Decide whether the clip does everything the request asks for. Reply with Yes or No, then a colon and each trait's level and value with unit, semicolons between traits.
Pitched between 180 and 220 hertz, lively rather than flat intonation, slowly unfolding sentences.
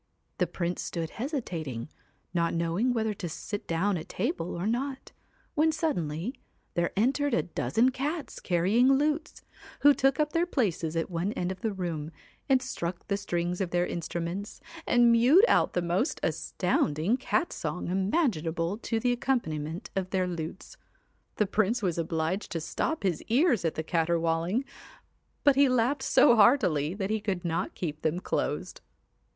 No: high, 190 Hz; wide, 6.9 semitones; average, 160 wpm